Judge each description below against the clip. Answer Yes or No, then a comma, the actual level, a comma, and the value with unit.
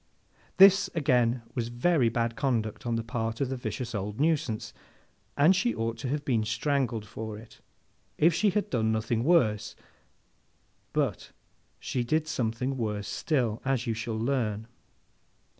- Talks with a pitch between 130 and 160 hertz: No, low, 120 Hz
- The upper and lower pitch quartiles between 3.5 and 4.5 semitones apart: Yes, average, 3.8 semitones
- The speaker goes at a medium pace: Yes, average, 150 wpm